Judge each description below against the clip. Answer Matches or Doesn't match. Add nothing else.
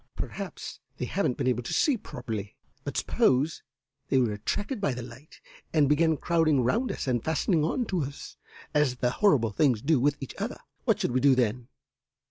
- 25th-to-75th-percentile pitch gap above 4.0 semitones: Matches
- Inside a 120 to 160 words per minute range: Doesn't match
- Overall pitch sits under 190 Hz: Matches